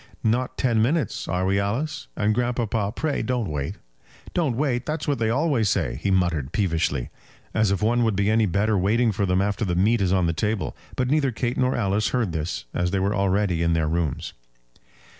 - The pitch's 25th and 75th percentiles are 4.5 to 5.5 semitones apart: Yes, average, 4.8 semitones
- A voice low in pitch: Yes, low, 105 Hz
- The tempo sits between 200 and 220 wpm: Yes, fast, 205 wpm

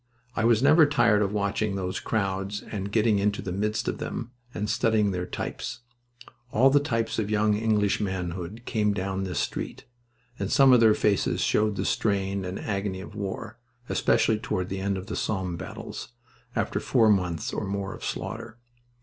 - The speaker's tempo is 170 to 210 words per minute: Yes, average, 180 wpm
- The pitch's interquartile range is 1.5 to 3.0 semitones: Yes, narrow, 2.4 semitones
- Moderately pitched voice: No, low, 105 Hz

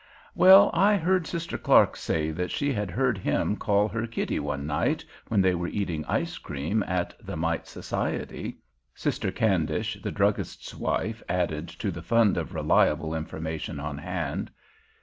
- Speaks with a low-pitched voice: Yes, very low, 90 Hz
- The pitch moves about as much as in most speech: No, wide, 6.1 semitones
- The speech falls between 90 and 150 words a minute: No, average, 160 wpm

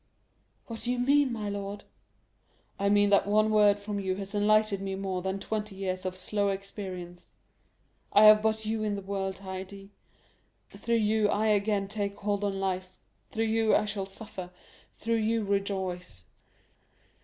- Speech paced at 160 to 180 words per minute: Yes, average, 165 wpm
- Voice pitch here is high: Yes, high, 200 Hz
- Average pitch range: No, narrow, 1.8 semitones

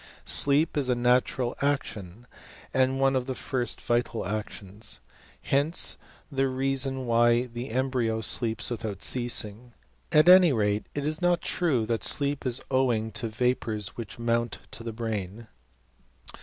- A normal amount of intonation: Yes, average, 3.2 semitones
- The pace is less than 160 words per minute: Yes, average, 140 wpm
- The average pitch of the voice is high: No, low, 120 Hz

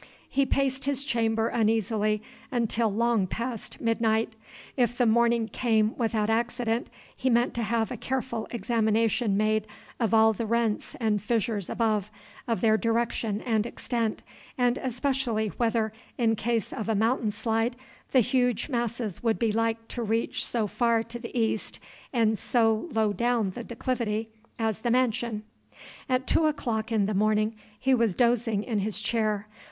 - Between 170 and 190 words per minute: No, average, 155 wpm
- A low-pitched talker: No, high, 230 Hz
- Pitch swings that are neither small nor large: No, narrow, 1.6 semitones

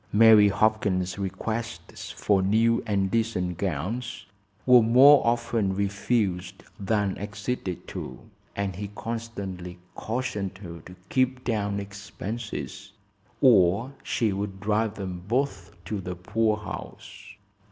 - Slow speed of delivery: Yes, slow, 115 wpm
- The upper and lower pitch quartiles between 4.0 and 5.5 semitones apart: No, average, 3.1 semitones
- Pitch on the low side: Yes, low, 105 Hz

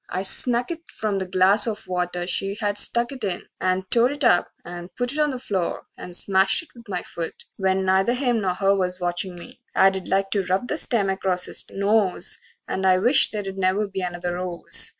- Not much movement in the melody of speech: No, average, 3.5 semitones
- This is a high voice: Yes, high, 195 Hz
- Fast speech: Yes, fast, 215 wpm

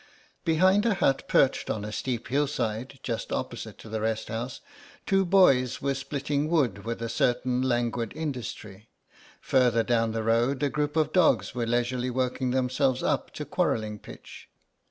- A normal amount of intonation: Yes, average, 3.6 semitones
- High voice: No, low, 125 Hz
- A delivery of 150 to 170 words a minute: Yes, average, 160 wpm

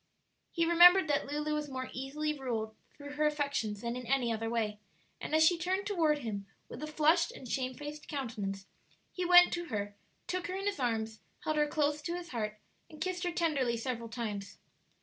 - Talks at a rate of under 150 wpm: No, average, 195 wpm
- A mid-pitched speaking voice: No, very high, 290 Hz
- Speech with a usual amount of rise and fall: No, wide, 6.1 semitones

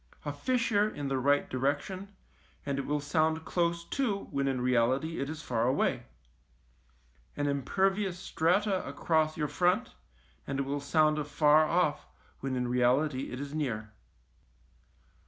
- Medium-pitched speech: Yes, medium, 150 Hz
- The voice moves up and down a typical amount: Yes, average, 3.7 semitones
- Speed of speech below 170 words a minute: Yes, average, 145 wpm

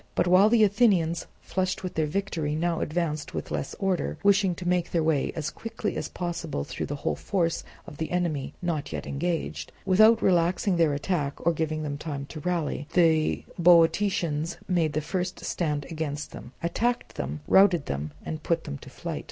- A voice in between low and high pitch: Yes, medium, 170 Hz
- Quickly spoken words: No, average, 185 wpm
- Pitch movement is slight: No, average, 3.2 semitones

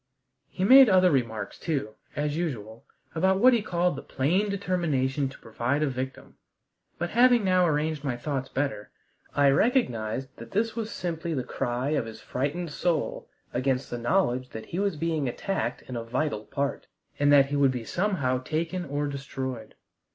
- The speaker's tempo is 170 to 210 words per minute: Yes, average, 175 wpm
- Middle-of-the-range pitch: Yes, medium, 145 Hz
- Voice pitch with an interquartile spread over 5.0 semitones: Yes, wide, 5.6 semitones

